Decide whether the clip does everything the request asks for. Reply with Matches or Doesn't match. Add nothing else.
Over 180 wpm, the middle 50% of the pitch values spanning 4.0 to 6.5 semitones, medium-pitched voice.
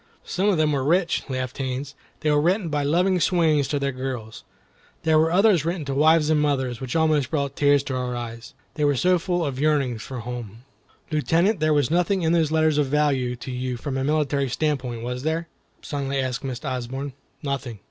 Doesn't match